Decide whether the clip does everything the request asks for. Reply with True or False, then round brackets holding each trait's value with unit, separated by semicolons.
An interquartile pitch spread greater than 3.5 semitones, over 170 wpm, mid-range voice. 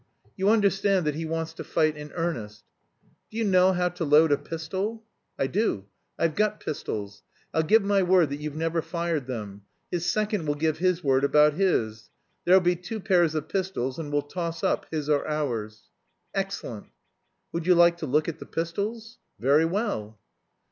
True (4.2 semitones; 180 wpm; 165 Hz)